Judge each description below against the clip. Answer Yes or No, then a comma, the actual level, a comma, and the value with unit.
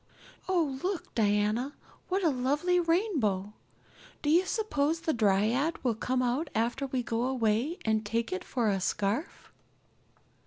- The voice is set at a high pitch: Yes, very high, 255 Hz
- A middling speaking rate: Yes, average, 145 wpm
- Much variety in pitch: Yes, wide, 6.7 semitones